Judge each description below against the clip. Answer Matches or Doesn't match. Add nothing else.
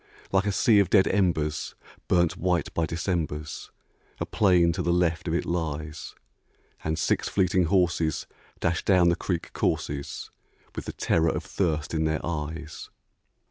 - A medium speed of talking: Matches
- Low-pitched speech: Matches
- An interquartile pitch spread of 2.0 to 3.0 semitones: Matches